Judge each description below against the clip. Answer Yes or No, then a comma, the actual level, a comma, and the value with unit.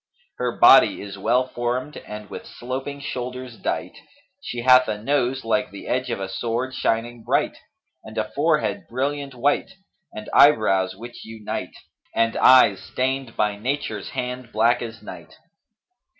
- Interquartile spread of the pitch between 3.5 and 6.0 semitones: No, narrow, 2.6 semitones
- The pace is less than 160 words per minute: Yes, average, 150 wpm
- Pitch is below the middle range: Yes, low, 120 Hz